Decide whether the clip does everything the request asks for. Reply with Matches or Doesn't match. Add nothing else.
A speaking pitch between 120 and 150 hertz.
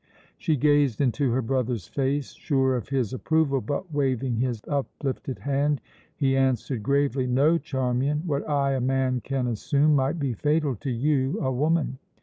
Matches